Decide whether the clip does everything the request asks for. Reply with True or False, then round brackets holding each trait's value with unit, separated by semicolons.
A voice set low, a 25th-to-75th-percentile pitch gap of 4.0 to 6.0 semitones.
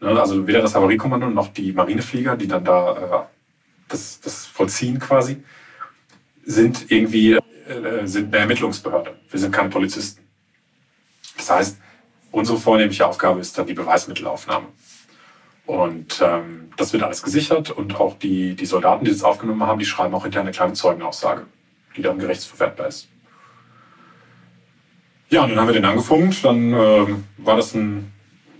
True (110 Hz; 4.6 semitones)